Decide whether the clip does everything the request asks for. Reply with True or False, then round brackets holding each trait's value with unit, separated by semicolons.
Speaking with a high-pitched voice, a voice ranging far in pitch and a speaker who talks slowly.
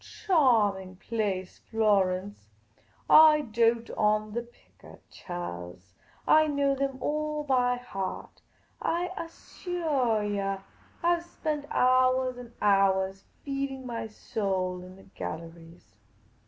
True (230 Hz; 6.3 semitones; 110 wpm)